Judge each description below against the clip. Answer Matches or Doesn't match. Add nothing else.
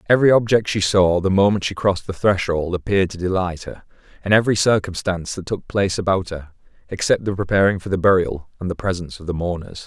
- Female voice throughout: Doesn't match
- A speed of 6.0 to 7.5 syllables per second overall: Matches